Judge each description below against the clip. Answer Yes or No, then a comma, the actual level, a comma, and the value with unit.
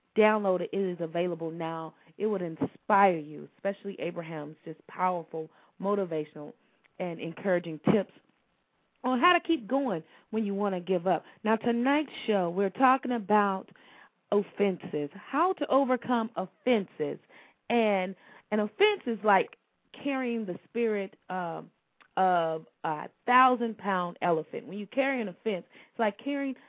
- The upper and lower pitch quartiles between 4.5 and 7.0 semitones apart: Yes, average, 5.1 semitones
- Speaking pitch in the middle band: No, high, 200 Hz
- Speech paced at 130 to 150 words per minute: Yes, average, 140 wpm